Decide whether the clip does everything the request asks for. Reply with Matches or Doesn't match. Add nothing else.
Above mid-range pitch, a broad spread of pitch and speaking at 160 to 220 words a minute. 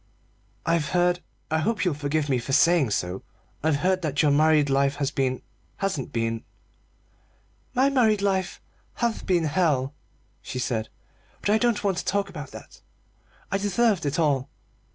Doesn't match